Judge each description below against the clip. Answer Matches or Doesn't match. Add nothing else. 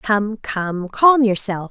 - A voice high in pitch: Matches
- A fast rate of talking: Doesn't match